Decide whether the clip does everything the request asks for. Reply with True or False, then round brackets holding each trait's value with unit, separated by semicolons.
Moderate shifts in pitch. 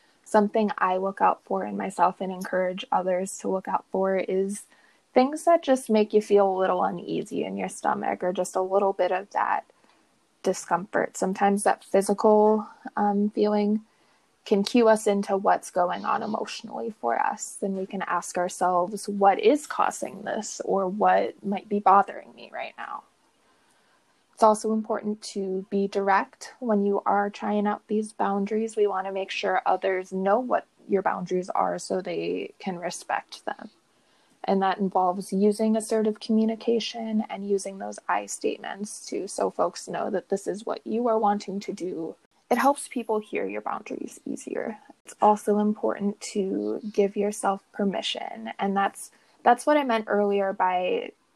False (2.1 semitones)